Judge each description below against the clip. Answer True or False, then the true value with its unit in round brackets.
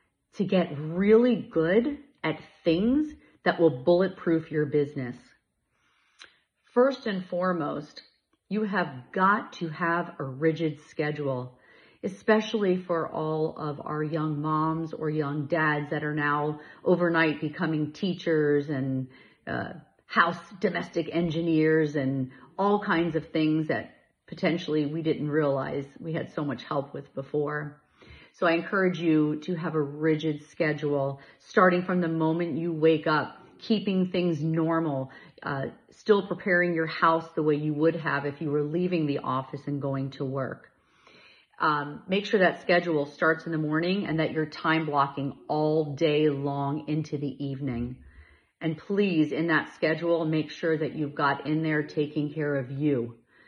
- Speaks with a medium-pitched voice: True (155 Hz)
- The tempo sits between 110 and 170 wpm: True (150 wpm)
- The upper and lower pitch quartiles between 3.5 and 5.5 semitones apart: False (2.6 semitones)